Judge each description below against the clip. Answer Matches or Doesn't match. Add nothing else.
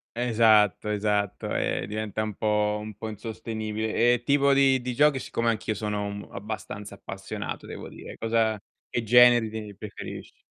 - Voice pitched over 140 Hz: Doesn't match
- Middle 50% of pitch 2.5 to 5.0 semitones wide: Doesn't match